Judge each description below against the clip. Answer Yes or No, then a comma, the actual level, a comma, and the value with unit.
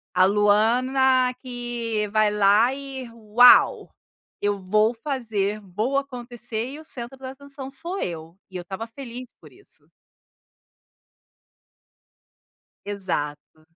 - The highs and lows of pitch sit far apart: No, average, 4.0 semitones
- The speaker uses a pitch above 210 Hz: Yes, high, 230 Hz